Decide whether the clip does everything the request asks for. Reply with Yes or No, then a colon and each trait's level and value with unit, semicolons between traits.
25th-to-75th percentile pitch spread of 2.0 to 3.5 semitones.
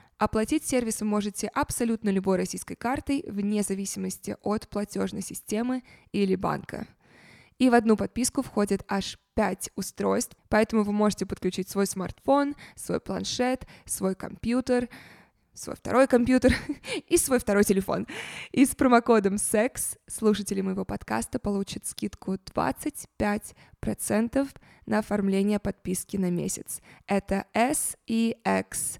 No: average, 4.1 semitones